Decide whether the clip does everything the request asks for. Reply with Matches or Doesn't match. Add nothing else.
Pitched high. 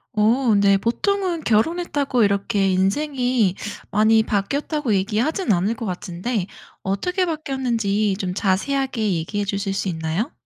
Matches